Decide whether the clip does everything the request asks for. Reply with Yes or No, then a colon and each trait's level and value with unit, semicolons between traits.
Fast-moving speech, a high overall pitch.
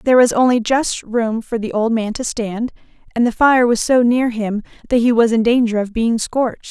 Yes: fast, 235 wpm; high, 230 Hz